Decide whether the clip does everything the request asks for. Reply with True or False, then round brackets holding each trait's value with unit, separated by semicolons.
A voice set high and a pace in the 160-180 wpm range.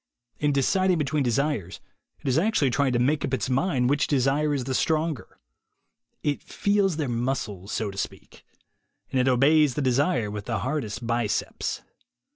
False (135 Hz; 165 wpm)